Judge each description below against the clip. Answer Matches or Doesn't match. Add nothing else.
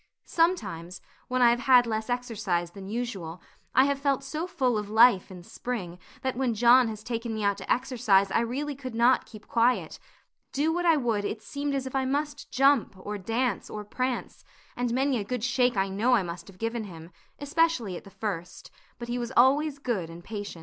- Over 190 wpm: Matches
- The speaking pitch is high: Matches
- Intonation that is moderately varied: Matches